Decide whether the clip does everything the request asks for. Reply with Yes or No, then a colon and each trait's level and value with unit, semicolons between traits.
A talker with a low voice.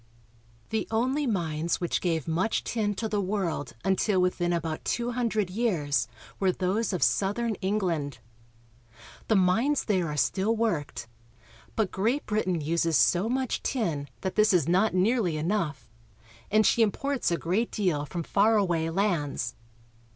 No: high, 190 Hz